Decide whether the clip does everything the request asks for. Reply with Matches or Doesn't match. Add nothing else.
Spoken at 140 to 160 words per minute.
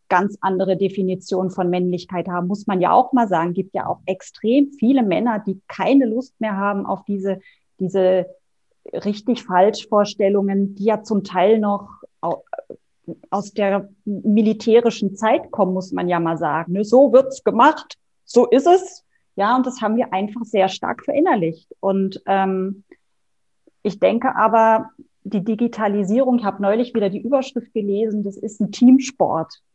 Matches